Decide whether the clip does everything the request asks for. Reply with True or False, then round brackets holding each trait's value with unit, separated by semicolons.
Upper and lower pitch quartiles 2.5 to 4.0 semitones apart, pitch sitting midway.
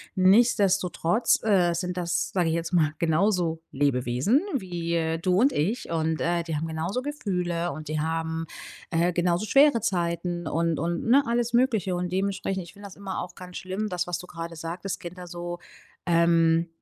True (2.8 semitones; 175 Hz)